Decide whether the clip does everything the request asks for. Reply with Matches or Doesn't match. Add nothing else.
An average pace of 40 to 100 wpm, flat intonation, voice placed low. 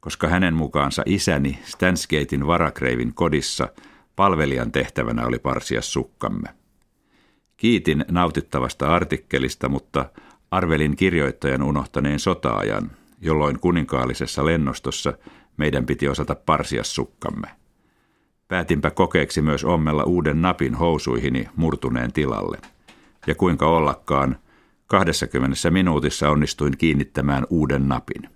Doesn't match